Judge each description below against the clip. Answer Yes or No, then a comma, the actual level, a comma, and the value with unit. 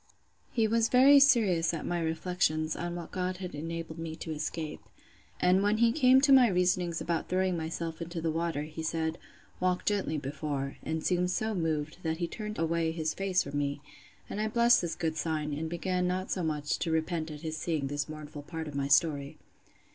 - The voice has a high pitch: No, medium, 165 Hz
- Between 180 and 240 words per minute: Yes, average, 200 wpm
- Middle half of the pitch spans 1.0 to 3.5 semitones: Yes, average, 2.8 semitones